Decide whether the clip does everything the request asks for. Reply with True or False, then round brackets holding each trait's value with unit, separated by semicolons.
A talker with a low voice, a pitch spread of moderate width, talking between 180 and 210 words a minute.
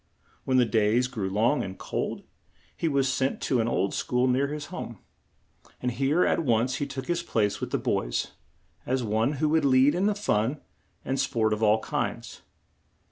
True (130 Hz; 4.1 semitones; 185 wpm)